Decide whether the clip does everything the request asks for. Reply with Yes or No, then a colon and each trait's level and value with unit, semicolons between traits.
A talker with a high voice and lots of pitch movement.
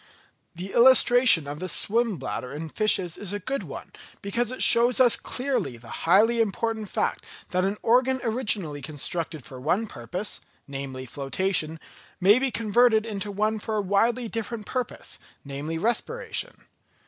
Yes: high, 205 Hz; wide, 6.3 semitones